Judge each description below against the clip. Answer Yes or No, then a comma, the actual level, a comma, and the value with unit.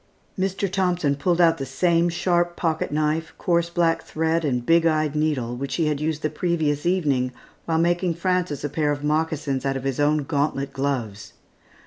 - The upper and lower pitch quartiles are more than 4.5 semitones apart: No, average, 3.2 semitones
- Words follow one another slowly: No, average, 180 wpm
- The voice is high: No, medium, 155 Hz